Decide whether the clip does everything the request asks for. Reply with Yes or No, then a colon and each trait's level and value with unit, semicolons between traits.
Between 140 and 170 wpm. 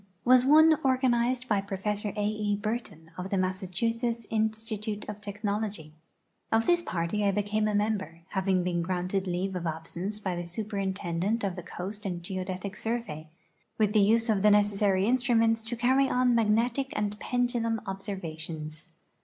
Yes: average, 165 wpm